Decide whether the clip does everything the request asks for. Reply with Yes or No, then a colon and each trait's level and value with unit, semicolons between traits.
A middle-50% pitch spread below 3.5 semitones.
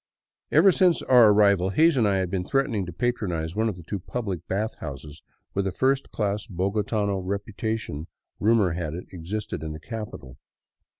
No: average, 3.9 semitones